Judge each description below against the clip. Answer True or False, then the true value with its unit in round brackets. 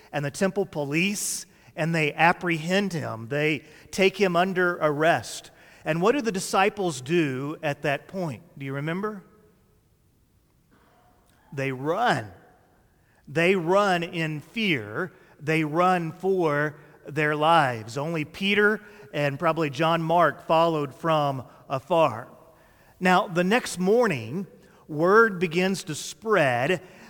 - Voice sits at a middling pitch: True (165 Hz)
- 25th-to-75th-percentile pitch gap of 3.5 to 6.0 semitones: True (3.8 semitones)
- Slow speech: True (115 wpm)